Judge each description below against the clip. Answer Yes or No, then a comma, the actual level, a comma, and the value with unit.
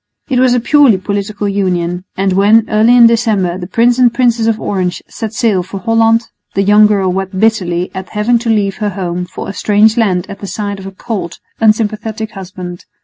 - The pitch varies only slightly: No, average, 3.1 semitones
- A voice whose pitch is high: Yes, high, 210 Hz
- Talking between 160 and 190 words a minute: No, fast, 205 wpm